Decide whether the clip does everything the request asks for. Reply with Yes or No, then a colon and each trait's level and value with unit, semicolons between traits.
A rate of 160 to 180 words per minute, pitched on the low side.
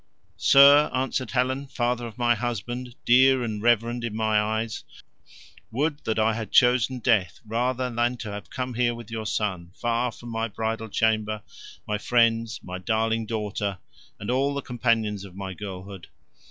Yes: average, 165 wpm; low, 115 Hz